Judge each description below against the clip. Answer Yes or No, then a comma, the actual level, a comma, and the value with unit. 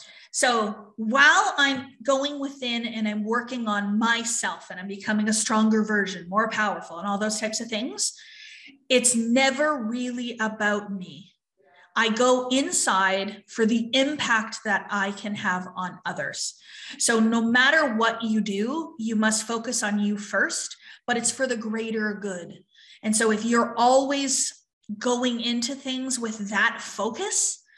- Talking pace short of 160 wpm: Yes, average, 150 wpm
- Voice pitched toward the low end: No, high, 230 Hz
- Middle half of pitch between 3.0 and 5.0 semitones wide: Yes, average, 3.8 semitones